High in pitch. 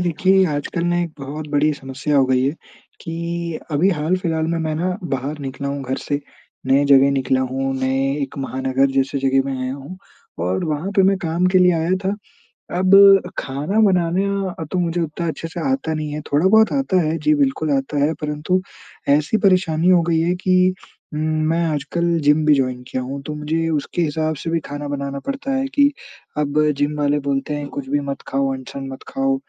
No: medium, 155 Hz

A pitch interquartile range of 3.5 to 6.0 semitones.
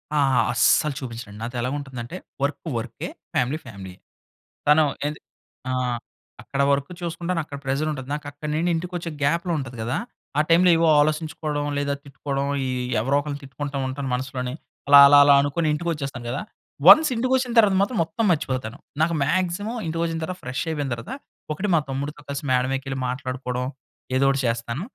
Yes: average, 4.2 semitones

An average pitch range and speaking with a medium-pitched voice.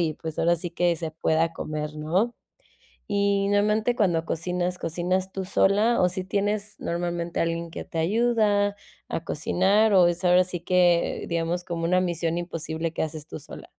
Yes: average, 3.1 semitones; medium, 175 Hz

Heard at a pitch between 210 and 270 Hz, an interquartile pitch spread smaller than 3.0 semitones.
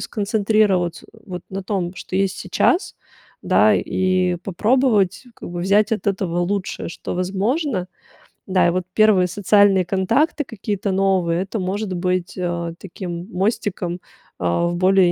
No: high, 190 Hz; narrow, 2.5 semitones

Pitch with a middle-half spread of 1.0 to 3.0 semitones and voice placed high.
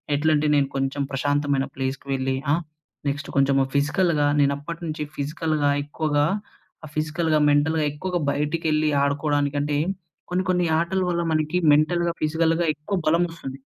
No: narrow, 2.4 semitones; medium, 150 Hz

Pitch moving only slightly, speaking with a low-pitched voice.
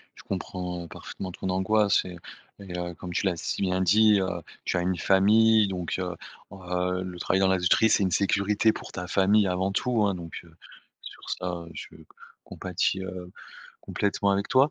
Yes: narrow, 1.9 semitones; very low, 95 Hz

